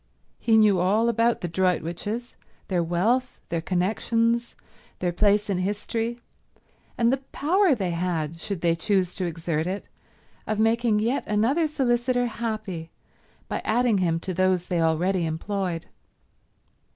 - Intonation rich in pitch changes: No, average, 4.8 semitones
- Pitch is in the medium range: No, high, 200 Hz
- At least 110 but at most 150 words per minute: Yes, average, 140 wpm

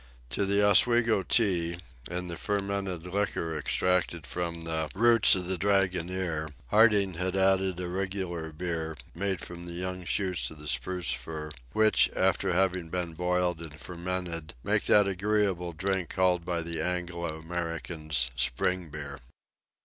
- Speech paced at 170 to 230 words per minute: No, average, 145 wpm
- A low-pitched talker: Yes, very low, 90 Hz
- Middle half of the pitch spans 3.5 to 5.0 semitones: No, narrow, 2.5 semitones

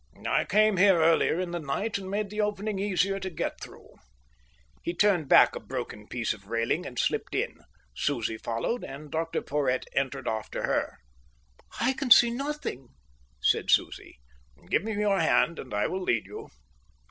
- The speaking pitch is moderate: Yes, medium, 175 Hz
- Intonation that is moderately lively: No, wide, 7.5 semitones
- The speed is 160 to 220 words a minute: Yes, average, 170 wpm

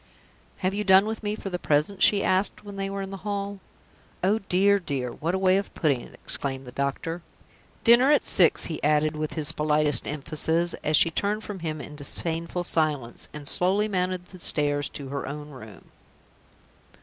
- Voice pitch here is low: No, medium, 170 Hz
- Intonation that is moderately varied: Yes, average, 4.8 semitones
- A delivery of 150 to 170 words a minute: No, average, 190 wpm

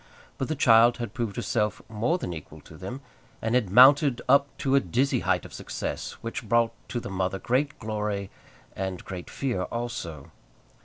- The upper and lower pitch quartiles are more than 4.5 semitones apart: Yes, average, 4.9 semitones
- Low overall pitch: Yes, low, 115 Hz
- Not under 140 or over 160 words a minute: No, average, 175 wpm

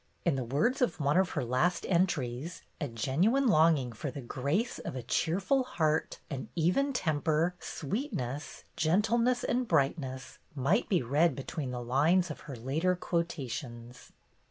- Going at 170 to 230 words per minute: No, average, 150 wpm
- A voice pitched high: No, medium, 155 Hz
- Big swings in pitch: Yes, wide, 5.7 semitones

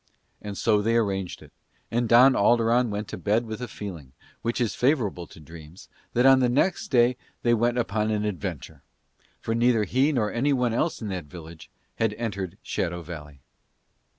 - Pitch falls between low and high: No, low, 110 Hz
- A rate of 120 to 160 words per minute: No, average, 175 wpm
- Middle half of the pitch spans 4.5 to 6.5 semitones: No, average, 4.0 semitones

